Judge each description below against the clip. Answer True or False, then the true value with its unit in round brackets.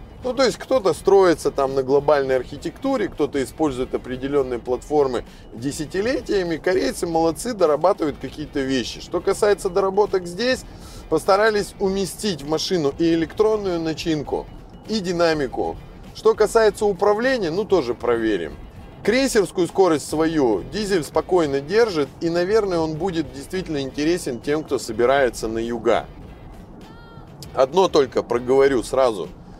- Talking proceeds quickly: False (120 wpm)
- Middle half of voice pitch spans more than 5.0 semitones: True (5.6 semitones)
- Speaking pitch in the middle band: True (165 Hz)